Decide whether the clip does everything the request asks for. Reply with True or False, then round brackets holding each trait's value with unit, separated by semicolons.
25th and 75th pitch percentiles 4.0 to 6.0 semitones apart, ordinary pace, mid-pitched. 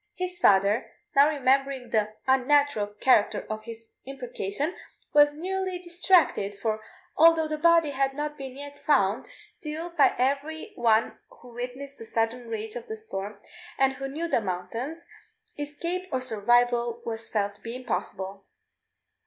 False (5.1 semitones; 145 wpm; 255 Hz)